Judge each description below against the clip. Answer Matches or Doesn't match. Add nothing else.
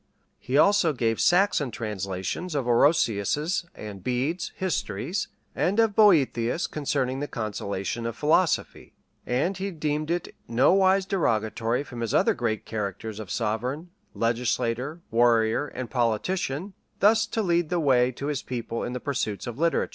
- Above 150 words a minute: Doesn't match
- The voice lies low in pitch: Matches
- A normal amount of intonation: Doesn't match